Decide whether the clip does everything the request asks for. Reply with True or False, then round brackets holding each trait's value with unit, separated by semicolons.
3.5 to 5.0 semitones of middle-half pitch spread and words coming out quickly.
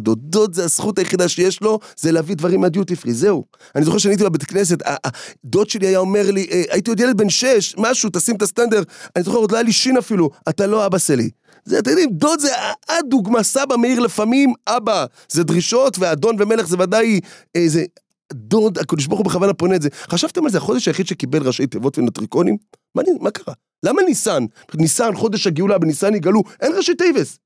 True (4.5 semitones; 190 wpm)